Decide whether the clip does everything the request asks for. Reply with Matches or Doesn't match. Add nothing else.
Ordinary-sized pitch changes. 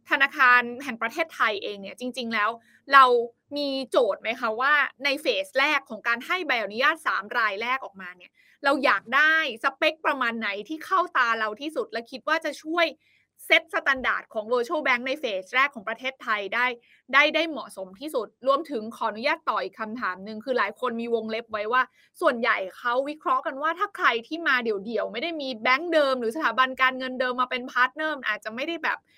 Matches